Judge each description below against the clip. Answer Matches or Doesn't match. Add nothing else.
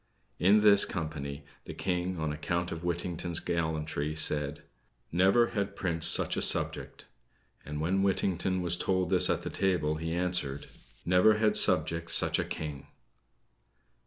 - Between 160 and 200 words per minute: Doesn't match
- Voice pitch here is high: Doesn't match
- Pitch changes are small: Doesn't match